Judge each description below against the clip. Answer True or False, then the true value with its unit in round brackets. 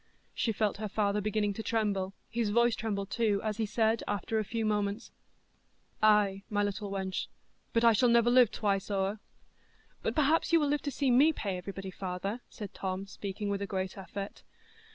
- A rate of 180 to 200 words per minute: True (190 wpm)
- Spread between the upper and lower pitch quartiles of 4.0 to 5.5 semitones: False (2.6 semitones)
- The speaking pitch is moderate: False (210 Hz)